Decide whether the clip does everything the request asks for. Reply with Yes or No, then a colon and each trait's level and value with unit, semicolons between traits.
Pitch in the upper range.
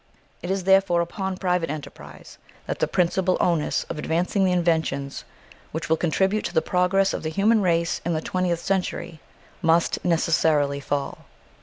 No: medium, 175 Hz